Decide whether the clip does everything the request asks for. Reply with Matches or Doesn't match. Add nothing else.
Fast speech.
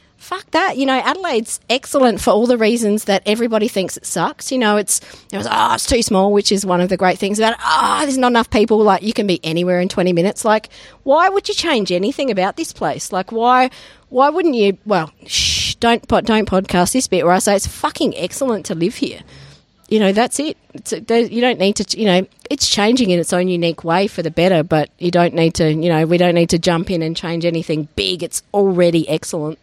Matches